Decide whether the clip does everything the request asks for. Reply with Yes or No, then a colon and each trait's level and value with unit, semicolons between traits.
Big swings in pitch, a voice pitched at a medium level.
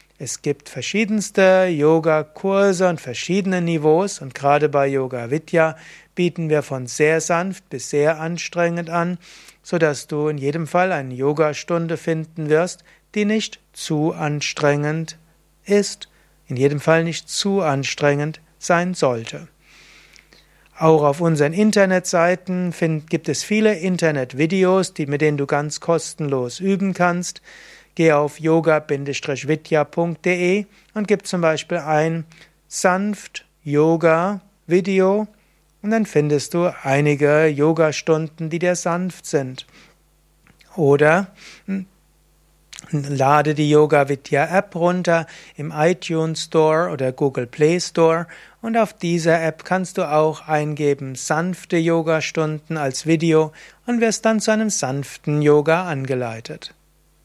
No: average, 3.3 semitones; medium, 160 Hz